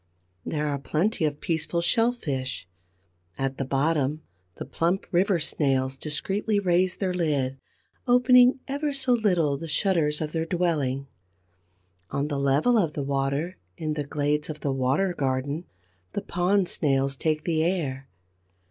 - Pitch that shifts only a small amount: No, average, 4.8 semitones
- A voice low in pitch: No, medium, 155 Hz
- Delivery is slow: No, average, 145 wpm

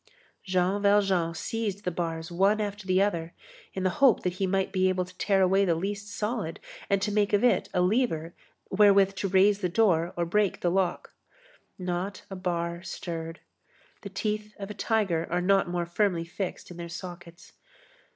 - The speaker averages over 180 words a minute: Yes, average, 190 wpm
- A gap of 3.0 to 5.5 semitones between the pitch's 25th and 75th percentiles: No, narrow, 2.6 semitones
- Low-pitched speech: No, high, 190 Hz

